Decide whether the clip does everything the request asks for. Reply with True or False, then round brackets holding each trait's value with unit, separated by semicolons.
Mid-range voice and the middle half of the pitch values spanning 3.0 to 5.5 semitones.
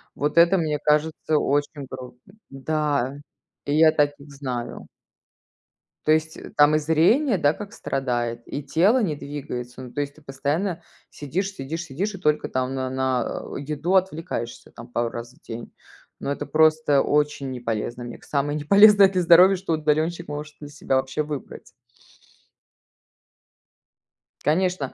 True (150 Hz; 3.4 semitones)